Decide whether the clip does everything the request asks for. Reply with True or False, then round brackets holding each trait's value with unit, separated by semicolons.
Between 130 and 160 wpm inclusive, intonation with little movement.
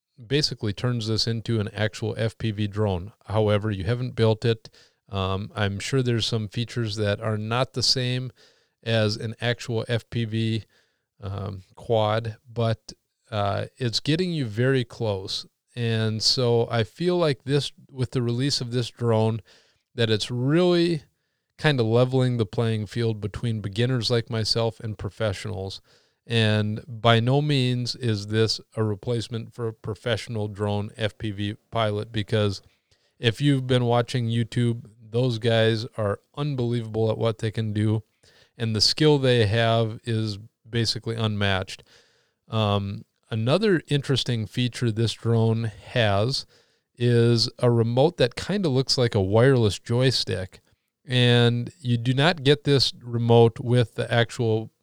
True (140 wpm; 2.3 semitones)